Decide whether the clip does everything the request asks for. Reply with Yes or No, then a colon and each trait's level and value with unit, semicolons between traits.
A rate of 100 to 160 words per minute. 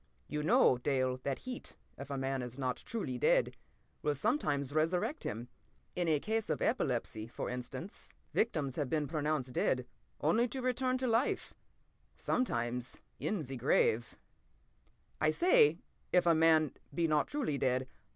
Yes: average, 150 wpm